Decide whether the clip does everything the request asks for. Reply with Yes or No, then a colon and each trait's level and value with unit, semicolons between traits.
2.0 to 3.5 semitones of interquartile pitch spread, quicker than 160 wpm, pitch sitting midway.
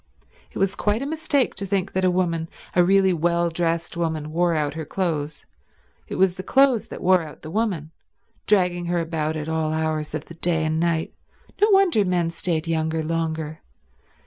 Yes: average, 2.9 semitones; average, 185 wpm; medium, 170 Hz